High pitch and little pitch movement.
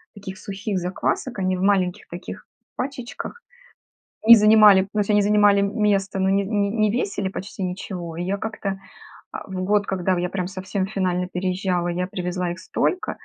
Yes: high, 195 Hz; narrow, 2.1 semitones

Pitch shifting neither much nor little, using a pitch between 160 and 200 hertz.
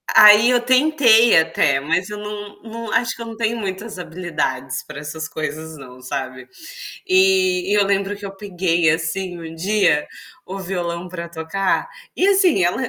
No: wide, 5.7 semitones; high, 190 Hz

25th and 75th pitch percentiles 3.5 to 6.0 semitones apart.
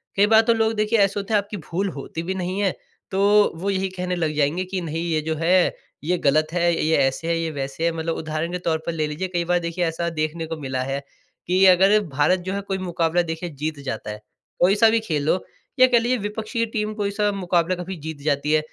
Yes: average, 3.9 semitones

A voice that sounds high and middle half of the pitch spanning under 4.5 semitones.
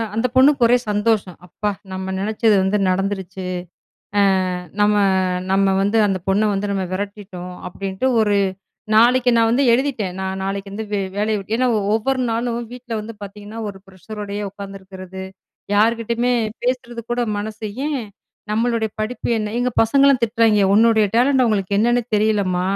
Yes: high, 215 Hz; average, 3.1 semitones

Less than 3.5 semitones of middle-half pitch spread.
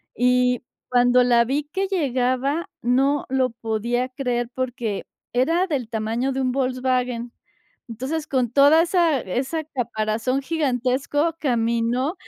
Yes: average, 2.7 semitones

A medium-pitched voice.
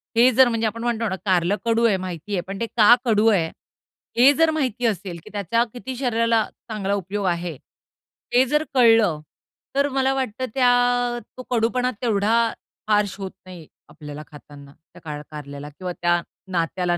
No: high, 210 Hz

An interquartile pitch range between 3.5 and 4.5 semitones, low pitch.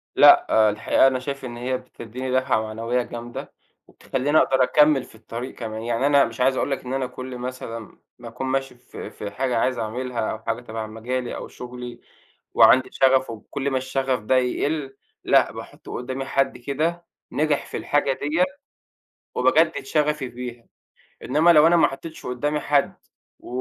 No: narrow, 2.5 semitones; low, 130 Hz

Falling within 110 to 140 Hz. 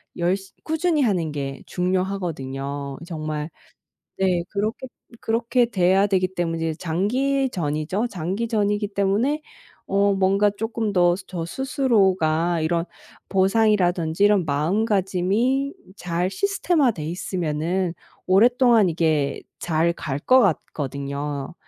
No: medium, 185 Hz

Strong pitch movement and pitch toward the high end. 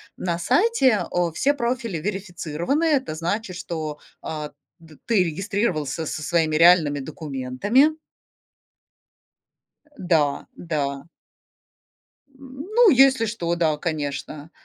No: wide, 7.4 semitones; medium, 175 Hz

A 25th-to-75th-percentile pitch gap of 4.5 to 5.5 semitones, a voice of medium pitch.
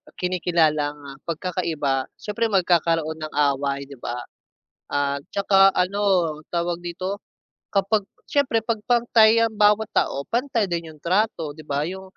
Yes: average, 5.2 semitones; medium, 175 Hz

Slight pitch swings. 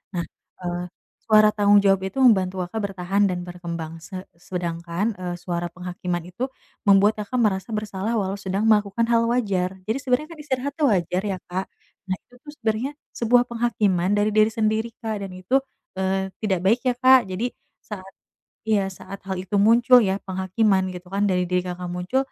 No: average, 3.4 semitones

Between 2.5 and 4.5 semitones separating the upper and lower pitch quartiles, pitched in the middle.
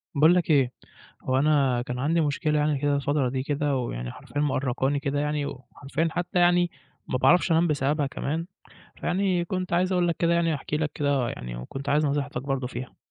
Yes: average, 3.6 semitones; medium, 145 Hz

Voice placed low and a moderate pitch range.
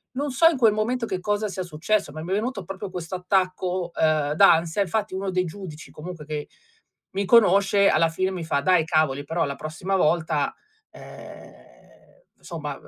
No: medium, 185 Hz; average, 3.9 semitones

